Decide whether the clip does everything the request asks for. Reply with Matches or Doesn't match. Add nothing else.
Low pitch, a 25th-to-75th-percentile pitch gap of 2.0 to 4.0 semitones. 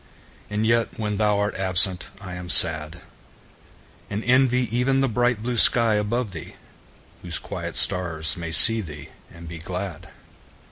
Doesn't match